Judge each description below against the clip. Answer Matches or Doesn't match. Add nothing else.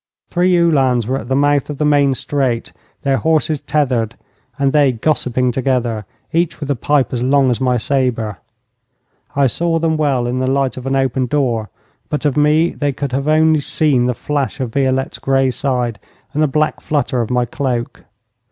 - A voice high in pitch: Doesn't match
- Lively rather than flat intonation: Doesn't match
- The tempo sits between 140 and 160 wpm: Doesn't match